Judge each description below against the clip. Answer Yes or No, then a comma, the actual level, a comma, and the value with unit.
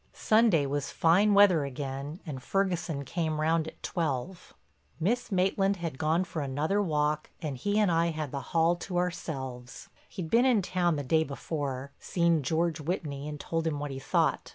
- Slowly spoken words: No, average, 175 wpm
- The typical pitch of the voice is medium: Yes, medium, 160 Hz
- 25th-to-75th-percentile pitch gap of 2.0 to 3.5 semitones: No, average, 3.9 semitones